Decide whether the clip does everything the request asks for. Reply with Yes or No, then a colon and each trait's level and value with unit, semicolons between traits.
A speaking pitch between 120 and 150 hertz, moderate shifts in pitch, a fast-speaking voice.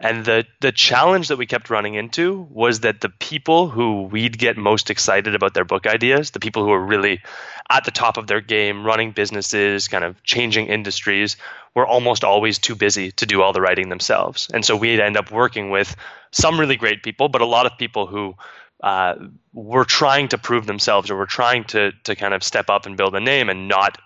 No: low, 110 Hz; average, 3.0 semitones; fast, 220 wpm